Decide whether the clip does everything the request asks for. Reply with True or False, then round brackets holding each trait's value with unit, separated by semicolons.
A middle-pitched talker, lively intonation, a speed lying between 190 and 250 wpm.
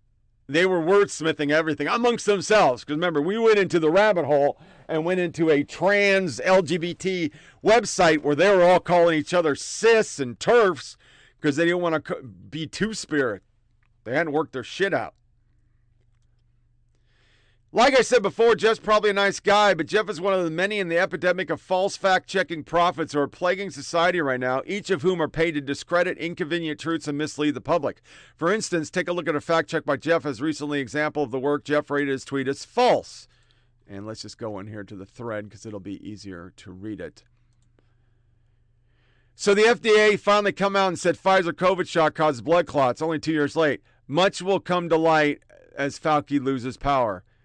True (155 Hz; 6.6 semitones; 195 wpm)